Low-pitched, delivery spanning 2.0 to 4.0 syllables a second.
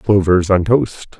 Yes: very low, 95 Hz; 3.7 syllables/s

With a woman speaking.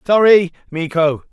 No: male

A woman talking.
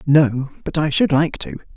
No: male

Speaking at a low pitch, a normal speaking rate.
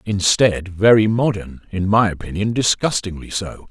No: low, 100 Hz; slow, 130 wpm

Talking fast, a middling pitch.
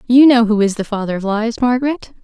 No: fast, 240 wpm; high, 230 Hz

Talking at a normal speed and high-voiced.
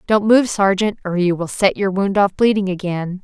No: fast, 220 wpm; high, 195 Hz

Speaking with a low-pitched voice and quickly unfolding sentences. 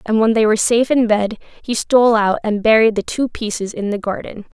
No: high, 220 Hz; fast, 235 wpm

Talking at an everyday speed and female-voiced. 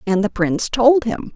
No: fast, 220 wpm; female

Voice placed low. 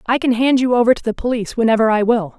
No: high, 235 Hz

